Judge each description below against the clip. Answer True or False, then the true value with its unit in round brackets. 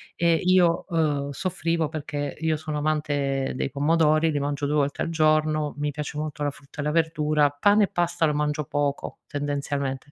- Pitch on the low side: False (150 Hz)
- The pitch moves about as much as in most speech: False (1.8 semitones)